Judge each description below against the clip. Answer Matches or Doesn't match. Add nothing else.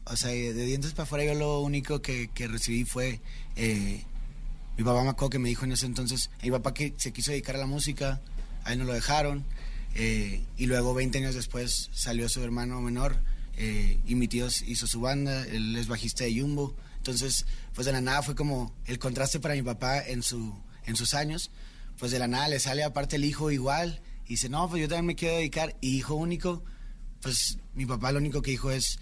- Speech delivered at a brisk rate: Matches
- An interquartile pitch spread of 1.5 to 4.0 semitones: Matches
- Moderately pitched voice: Doesn't match